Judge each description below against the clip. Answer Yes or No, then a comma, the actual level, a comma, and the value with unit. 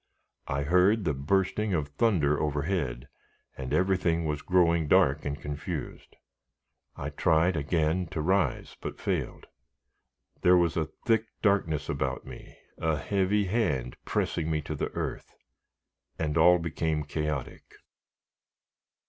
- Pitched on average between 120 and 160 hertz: No, very low, 80 Hz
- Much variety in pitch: No, average, 3.8 semitones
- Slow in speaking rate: Yes, slow, 125 wpm